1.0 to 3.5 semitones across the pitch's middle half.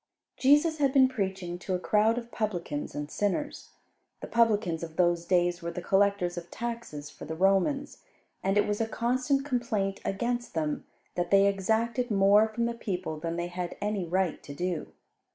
No: average, 5.0 semitones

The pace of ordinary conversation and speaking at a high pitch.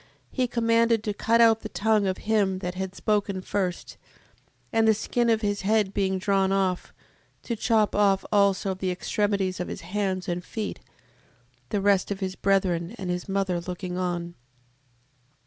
Yes: average, 165 wpm; high, 195 Hz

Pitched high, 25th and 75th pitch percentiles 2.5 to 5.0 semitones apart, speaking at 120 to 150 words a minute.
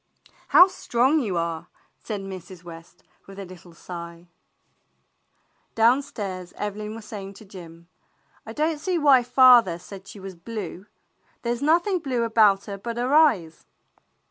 No: high, 210 Hz; wide, 5.4 semitones; average, 145 wpm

